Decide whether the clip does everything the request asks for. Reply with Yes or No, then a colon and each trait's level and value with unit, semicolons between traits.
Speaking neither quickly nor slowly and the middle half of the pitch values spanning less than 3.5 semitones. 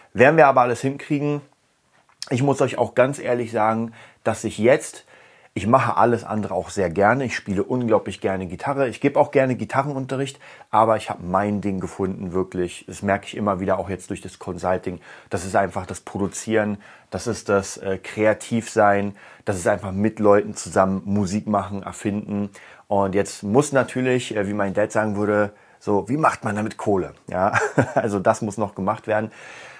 Yes: average, 180 wpm; average, 2.8 semitones